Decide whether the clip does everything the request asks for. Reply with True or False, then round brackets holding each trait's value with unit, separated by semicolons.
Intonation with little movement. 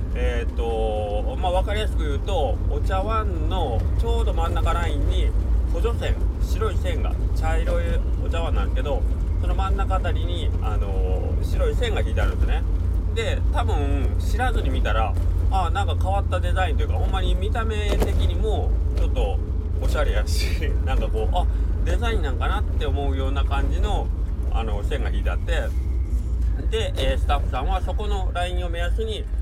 True (2.2 semitones)